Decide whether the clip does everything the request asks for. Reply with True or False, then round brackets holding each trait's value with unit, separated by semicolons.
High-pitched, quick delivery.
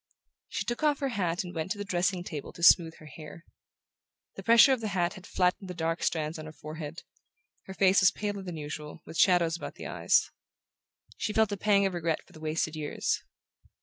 False (175 Hz; 215 wpm)